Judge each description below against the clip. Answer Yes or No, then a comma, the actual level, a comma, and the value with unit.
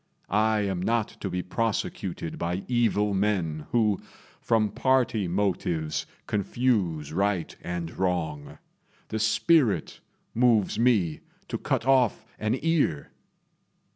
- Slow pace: Yes, slow, 110 wpm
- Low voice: Yes, low, 100 Hz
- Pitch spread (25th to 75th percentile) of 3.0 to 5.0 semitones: Yes, average, 4.6 semitones